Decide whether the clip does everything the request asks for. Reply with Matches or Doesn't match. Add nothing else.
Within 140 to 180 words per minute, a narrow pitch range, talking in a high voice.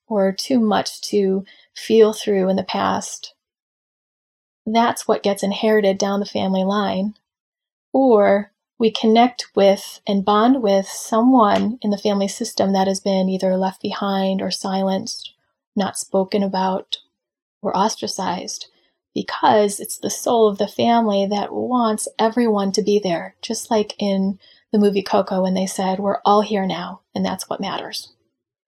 Matches